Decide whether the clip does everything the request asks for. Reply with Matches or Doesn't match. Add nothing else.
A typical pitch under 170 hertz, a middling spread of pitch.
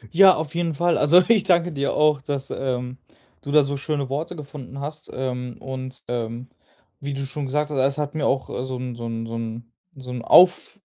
Matches